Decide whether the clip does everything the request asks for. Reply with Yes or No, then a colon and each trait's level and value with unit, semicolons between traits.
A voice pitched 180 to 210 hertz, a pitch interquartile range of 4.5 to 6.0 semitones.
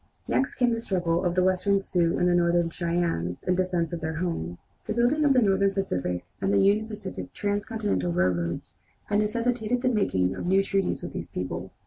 No: medium, 185 Hz; average, 4.0 semitones